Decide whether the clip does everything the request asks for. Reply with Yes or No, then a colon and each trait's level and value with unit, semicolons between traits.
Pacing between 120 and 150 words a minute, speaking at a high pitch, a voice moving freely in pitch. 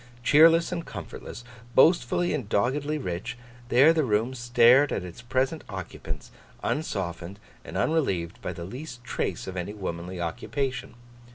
No: average, 140 wpm; low, 120 Hz; wide, 7.5 semitones